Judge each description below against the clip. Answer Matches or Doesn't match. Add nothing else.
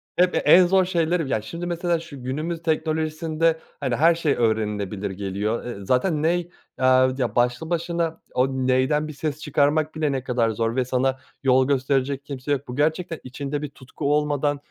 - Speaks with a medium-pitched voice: Matches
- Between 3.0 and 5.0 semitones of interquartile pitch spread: Matches